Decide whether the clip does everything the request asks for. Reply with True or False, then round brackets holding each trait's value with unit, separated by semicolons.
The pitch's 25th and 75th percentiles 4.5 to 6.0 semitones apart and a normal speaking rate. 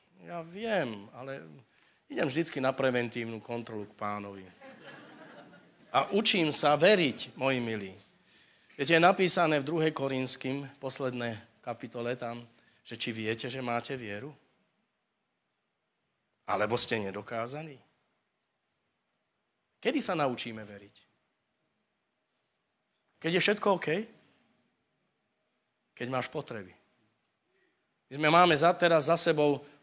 False (5.4 semitones; 105 wpm)